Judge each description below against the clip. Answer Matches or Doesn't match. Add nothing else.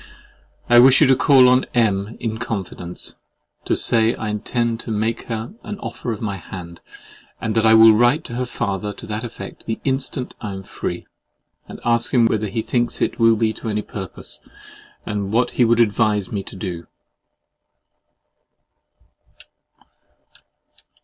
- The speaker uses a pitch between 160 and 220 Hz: Doesn't match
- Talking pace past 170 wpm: Doesn't match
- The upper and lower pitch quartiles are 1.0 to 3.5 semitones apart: Matches